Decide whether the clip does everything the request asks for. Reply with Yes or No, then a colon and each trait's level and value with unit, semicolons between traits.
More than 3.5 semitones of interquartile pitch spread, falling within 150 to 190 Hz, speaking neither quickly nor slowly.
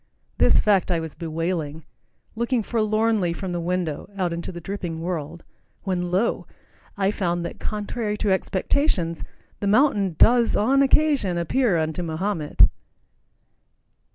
No: average, 4.2 semitones; medium, 185 Hz; slow, 130 wpm